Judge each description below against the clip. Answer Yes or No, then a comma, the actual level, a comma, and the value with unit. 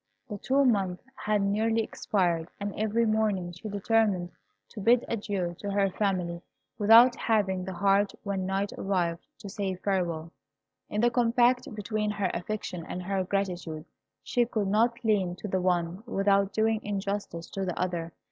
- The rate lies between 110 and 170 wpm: Yes, average, 160 wpm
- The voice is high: Yes, high, 200 Hz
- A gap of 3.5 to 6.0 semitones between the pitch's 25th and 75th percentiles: No, average, 2.9 semitones